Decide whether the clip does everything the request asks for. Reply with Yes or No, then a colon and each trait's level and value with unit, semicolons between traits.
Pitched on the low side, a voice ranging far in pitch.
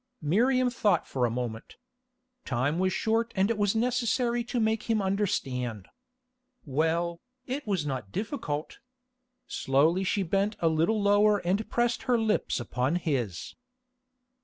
No: high, 195 Hz; wide, 7.4 semitones